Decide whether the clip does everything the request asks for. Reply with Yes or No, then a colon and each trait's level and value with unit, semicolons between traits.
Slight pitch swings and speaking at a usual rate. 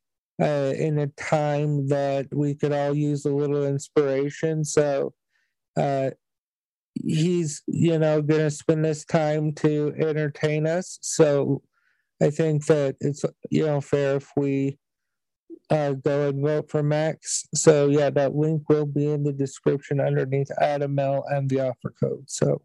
Yes: narrow, 1.5 semitones; average, 150 wpm